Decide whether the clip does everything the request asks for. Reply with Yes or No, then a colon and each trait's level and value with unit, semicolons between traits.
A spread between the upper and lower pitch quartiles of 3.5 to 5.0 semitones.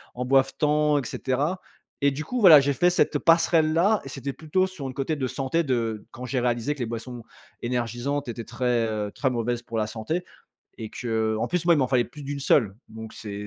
Yes: average, 4.2 semitones